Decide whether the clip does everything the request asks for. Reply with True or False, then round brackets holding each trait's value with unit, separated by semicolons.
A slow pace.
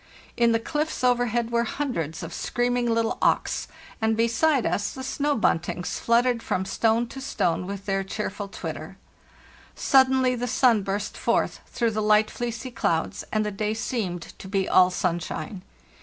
False (165 wpm)